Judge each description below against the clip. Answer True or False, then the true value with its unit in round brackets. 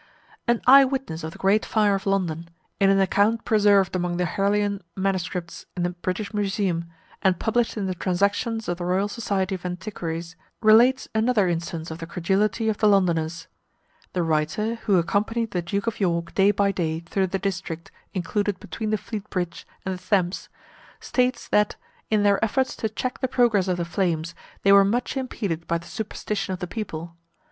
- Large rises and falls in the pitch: False (3.4 semitones)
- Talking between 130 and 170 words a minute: False (185 wpm)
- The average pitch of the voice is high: True (195 Hz)